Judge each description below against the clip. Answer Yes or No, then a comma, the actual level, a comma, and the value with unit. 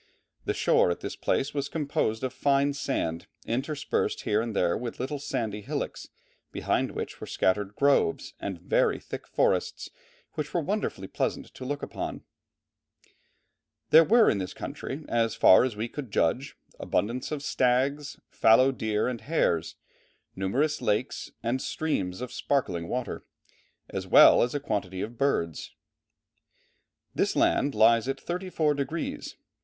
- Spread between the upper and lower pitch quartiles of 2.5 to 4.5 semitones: No, average, 5.2 semitones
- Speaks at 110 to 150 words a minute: Yes, average, 145 wpm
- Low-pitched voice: Yes, low, 125 Hz